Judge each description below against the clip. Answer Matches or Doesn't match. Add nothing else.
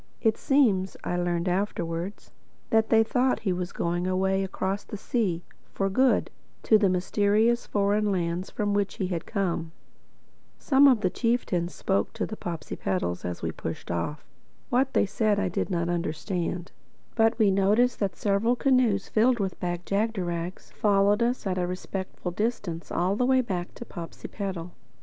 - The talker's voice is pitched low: Doesn't match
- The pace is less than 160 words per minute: Doesn't match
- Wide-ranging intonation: Doesn't match